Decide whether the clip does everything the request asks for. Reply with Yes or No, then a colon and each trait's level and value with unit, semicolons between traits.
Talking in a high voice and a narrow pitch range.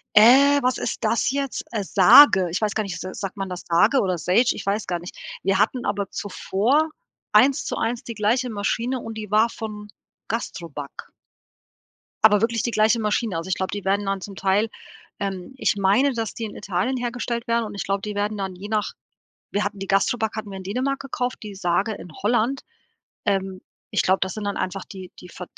No: high, 210 Hz; average, 3.3 semitones